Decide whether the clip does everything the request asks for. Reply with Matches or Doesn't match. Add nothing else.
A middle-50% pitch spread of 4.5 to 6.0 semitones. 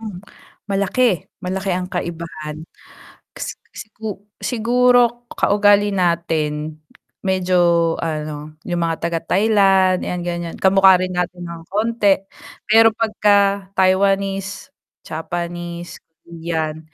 Doesn't match